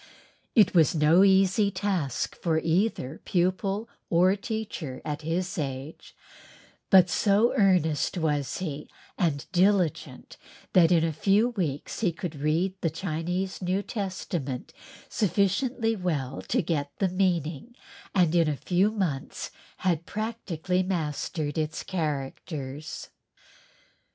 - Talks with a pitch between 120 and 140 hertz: No, medium, 175 Hz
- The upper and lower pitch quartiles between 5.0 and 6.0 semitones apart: No, average, 4.1 semitones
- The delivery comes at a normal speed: No, slow, 120 wpm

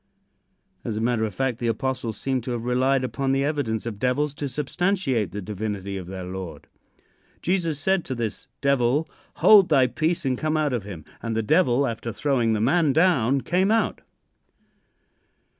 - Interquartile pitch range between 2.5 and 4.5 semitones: No, average, 5.1 semitones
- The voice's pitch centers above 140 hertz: No, low, 130 Hz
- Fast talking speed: No, average, 175 wpm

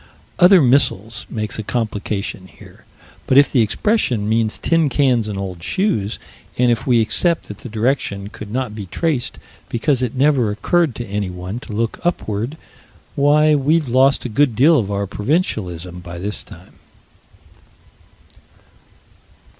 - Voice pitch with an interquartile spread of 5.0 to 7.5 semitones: Yes, wide, 5.4 semitones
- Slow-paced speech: No, average, 145 wpm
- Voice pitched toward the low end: Yes, low, 115 Hz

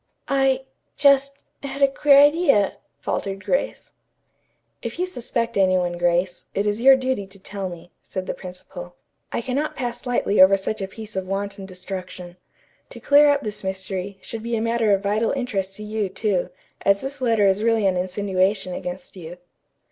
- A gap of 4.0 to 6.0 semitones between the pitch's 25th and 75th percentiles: Yes, average, 4.7 semitones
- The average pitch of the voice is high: Yes, high, 205 Hz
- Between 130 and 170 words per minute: No, average, 180 wpm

